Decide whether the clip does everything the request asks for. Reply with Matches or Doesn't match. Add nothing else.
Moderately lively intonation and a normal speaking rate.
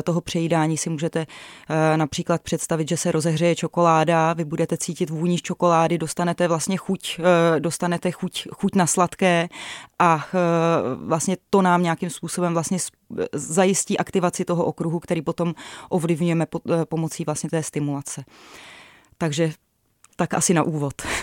Doesn't match